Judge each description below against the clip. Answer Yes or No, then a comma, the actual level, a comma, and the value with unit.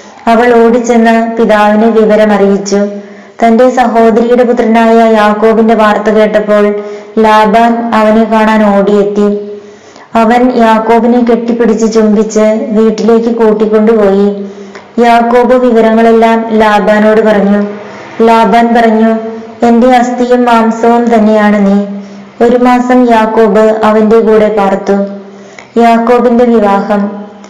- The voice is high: Yes, high, 220 Hz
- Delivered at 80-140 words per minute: Yes, average, 85 wpm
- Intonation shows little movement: Yes, narrow, 1.9 semitones